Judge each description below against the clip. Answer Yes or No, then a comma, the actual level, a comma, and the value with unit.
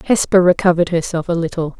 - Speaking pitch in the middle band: Yes, medium, 170 Hz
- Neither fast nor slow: Yes, average, 165 wpm